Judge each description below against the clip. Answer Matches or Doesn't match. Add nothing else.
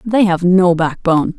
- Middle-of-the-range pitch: Matches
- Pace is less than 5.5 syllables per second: Matches